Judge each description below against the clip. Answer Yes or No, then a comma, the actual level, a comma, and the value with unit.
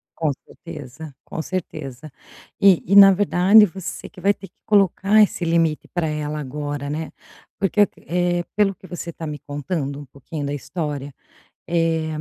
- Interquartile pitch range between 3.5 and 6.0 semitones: Yes, average, 4.2 semitones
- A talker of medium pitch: Yes, medium, 165 Hz